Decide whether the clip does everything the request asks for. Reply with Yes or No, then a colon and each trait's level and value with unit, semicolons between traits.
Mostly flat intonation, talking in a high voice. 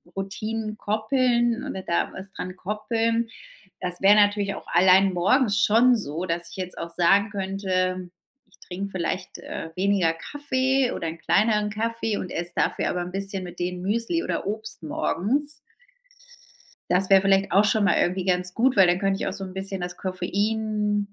No: average, 3.0 semitones; high, 195 Hz